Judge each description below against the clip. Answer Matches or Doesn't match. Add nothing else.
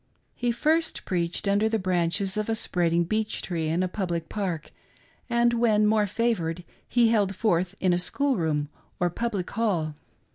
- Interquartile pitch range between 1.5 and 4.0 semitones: Doesn't match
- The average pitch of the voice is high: Matches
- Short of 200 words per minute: Matches